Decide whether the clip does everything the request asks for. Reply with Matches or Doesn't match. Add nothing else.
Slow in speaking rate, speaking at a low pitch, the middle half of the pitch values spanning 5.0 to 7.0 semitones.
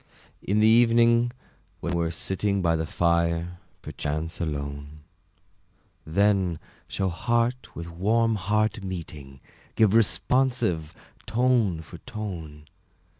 Matches